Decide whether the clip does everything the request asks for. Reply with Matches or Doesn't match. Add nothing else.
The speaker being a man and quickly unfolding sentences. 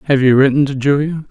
Matches